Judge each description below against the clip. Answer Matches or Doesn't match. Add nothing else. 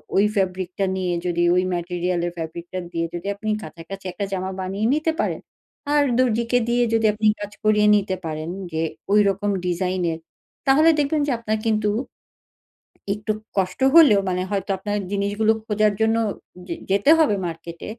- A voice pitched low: Doesn't match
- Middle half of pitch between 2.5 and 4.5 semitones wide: Matches